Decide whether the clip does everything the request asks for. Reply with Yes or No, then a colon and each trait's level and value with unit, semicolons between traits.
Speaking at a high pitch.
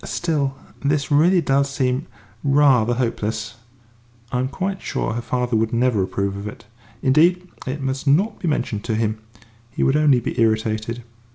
No: low, 130 Hz